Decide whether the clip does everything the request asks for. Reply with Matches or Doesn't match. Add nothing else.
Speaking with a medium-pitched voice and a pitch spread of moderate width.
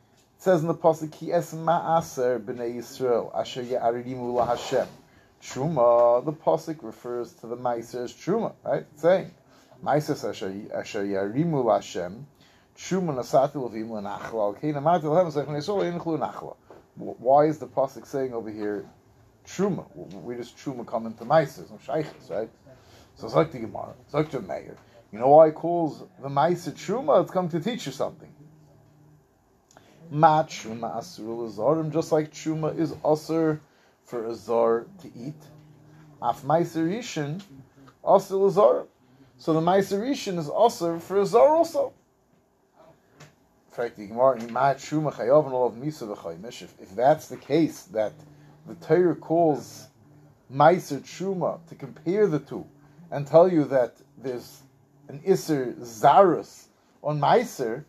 Matches